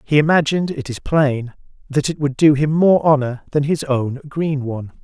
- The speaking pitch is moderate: Yes, medium, 145 Hz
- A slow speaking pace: No, average, 200 wpm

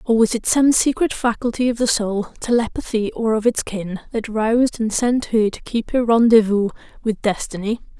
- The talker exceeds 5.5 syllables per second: No, 5.0 syllables/s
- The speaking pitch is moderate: No, high, 225 Hz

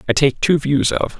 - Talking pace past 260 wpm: No, fast, 250 wpm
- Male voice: Yes, male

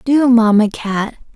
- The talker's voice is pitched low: No, high, 230 Hz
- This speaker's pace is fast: No, slow, 135 wpm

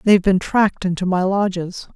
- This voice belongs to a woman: Yes, female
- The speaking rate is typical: No, fast, 215 wpm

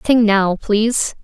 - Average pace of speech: Yes, average, 145 wpm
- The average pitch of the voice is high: Yes, high, 215 Hz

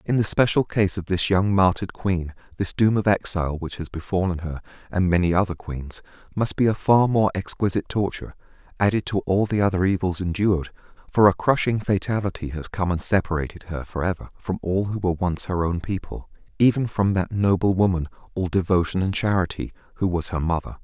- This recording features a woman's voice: No, male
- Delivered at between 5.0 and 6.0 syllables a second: Yes, 5.8 syllables/s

